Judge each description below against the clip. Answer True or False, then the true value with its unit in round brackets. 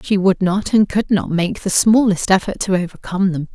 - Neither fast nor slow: False (220 wpm)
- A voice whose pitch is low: False (190 Hz)